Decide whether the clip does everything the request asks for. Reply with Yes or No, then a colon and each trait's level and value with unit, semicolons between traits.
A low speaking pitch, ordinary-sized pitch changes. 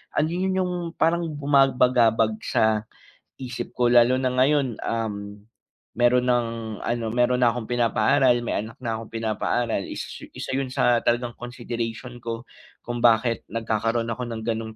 No: low, 120 Hz; narrow, 1.9 semitones